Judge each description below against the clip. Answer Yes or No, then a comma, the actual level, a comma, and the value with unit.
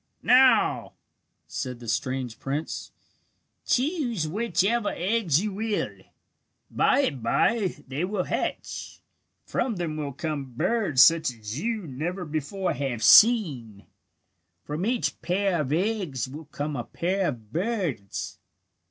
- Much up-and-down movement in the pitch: Yes, wide, 7.6 semitones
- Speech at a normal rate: No, slow, 125 wpm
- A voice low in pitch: No, medium, 165 Hz